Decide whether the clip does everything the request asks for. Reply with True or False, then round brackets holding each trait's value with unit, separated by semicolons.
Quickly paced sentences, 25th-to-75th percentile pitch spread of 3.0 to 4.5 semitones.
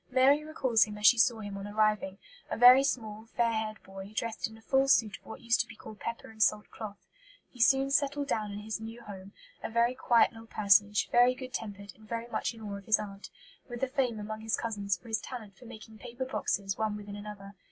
False (235 wpm; 2.5 semitones)